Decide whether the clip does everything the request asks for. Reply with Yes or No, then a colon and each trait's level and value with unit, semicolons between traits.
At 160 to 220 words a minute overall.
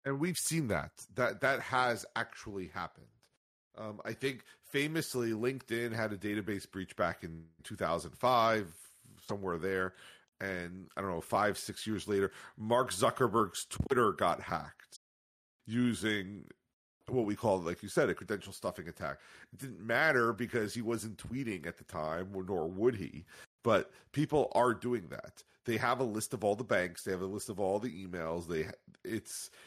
Yes: average, 170 wpm